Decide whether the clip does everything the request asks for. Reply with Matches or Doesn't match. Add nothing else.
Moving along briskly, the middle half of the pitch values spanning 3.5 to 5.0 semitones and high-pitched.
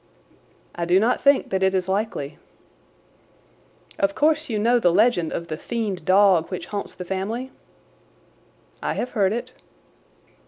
Doesn't match